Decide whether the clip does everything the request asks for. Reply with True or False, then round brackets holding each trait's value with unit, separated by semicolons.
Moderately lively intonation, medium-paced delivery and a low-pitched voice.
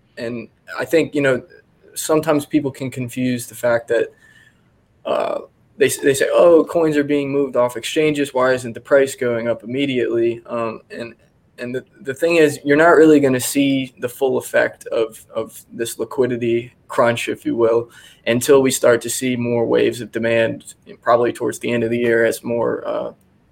True (3.7 semitones; 190 wpm; 130 Hz)